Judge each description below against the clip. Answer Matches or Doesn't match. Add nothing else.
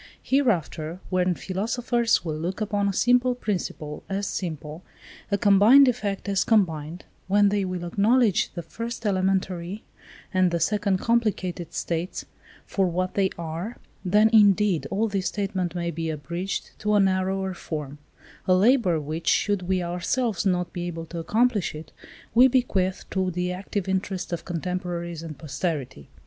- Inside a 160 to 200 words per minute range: Doesn't match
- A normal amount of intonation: Matches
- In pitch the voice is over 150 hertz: Matches